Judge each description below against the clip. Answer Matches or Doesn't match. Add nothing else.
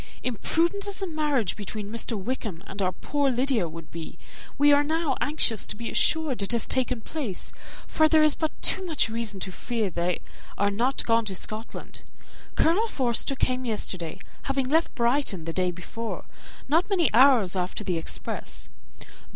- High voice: Matches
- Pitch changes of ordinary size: Doesn't match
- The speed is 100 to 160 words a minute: Doesn't match